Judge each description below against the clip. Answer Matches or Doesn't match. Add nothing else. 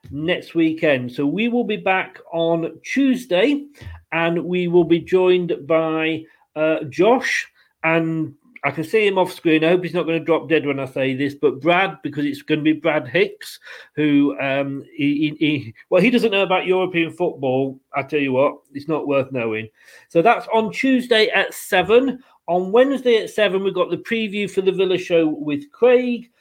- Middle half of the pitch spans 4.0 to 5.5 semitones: Matches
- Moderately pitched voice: Matches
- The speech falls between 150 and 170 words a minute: Doesn't match